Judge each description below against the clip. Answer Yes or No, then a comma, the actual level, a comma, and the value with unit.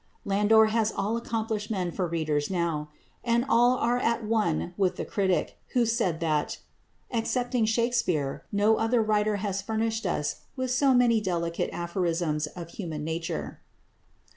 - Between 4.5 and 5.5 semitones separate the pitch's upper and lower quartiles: Yes, average, 5.1 semitones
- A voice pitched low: No, high, 210 Hz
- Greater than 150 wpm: No, average, 145 wpm